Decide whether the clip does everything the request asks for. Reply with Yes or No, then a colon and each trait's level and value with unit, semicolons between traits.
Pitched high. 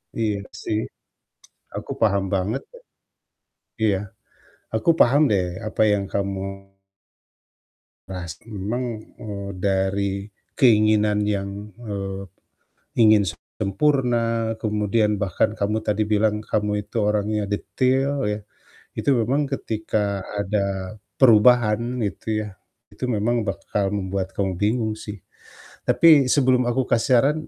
No: low, 105 Hz